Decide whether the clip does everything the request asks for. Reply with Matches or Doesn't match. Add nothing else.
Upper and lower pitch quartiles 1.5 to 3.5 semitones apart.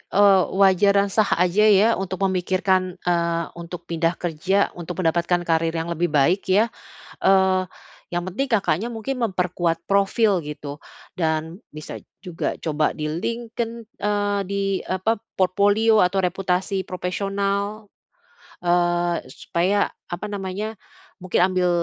Matches